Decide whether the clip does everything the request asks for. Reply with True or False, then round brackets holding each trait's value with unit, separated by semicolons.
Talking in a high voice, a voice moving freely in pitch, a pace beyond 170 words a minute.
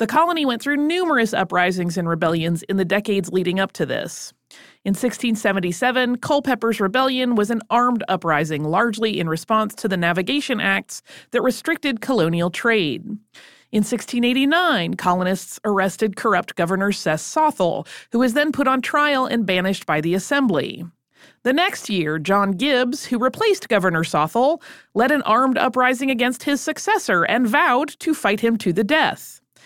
False (225 Hz; 5.7 semitones; 155 wpm)